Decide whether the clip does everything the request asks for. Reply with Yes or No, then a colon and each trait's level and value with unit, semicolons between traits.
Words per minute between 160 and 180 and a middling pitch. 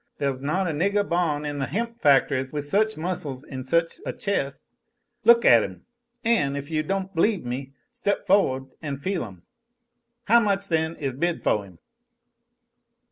Yes: average, 170 wpm; medium, 155 Hz